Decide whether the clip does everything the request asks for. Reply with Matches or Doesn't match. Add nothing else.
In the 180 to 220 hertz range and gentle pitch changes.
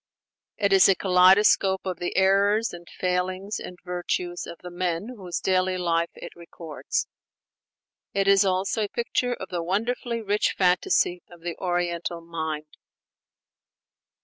Matches